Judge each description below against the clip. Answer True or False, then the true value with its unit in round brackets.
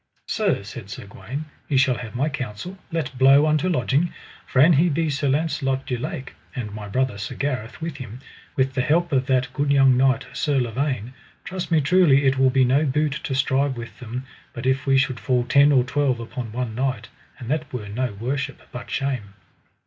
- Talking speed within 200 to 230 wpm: True (205 wpm)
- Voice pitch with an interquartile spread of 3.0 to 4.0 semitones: False (2.4 semitones)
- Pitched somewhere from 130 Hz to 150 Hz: True (135 Hz)